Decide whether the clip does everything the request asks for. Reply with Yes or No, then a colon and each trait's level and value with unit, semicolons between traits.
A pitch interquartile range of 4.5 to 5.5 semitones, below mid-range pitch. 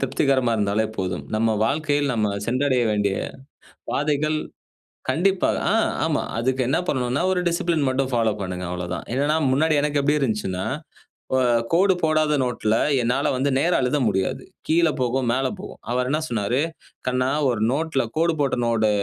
Yes: average, 5.0 semitones; low, 130 Hz